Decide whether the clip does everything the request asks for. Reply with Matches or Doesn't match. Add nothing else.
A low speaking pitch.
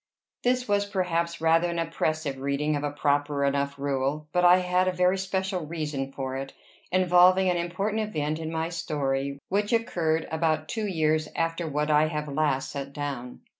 Doesn't match